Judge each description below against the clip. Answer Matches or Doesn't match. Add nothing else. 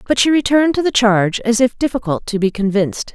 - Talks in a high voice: Matches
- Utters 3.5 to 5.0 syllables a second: Doesn't match